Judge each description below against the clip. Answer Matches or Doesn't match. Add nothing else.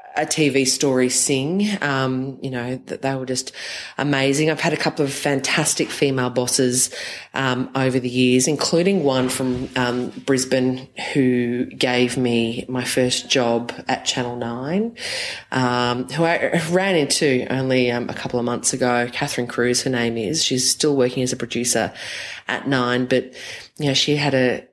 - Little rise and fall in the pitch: Matches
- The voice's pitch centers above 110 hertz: Matches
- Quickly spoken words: Doesn't match